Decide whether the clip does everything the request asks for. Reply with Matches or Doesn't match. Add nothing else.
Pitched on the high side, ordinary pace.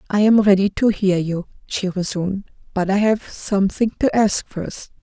Matches